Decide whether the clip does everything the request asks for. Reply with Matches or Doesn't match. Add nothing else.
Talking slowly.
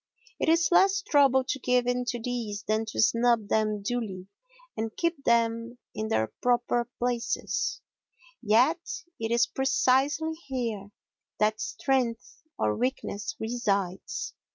Matches